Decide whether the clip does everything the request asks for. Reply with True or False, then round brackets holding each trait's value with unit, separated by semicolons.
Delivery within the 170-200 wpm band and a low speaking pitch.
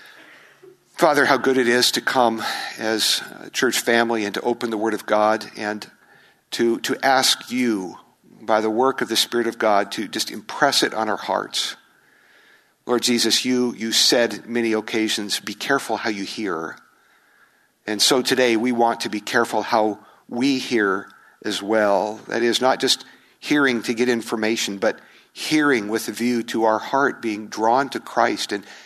True (175 wpm; 115 Hz)